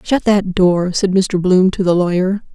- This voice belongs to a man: No, female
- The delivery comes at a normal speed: No, fast, 210 wpm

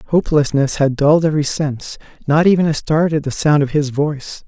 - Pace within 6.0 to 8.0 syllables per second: No, 5.8 syllables/s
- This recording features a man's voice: Yes, male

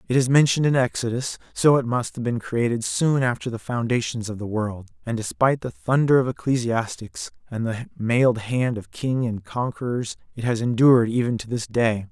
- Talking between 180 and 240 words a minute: Yes, average, 195 wpm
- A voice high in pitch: No, low, 120 Hz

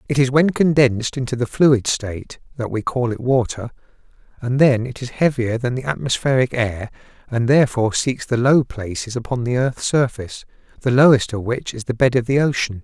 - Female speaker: No, male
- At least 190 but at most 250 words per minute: Yes, average, 195 wpm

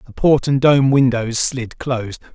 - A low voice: Yes, low, 130 Hz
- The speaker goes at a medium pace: Yes, average, 180 wpm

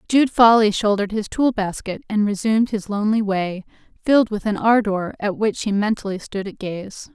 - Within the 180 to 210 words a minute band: Yes, average, 185 wpm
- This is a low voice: No, high, 210 Hz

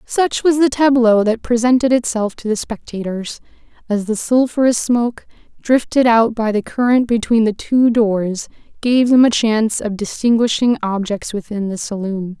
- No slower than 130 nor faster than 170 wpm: Yes, average, 160 wpm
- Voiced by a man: No, female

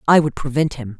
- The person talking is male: No, female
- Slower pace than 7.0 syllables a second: Yes, 6.0 syllables/s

